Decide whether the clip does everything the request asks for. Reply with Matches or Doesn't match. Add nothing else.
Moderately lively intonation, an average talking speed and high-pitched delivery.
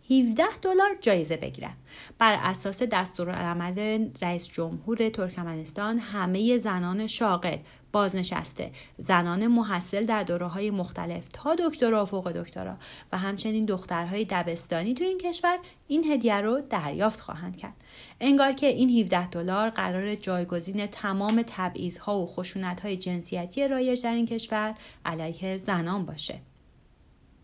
Doesn't match